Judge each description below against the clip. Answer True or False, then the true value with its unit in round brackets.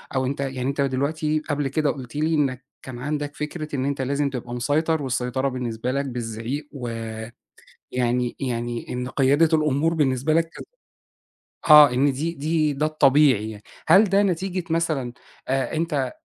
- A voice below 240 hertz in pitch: True (140 Hz)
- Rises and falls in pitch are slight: False (3.3 semitones)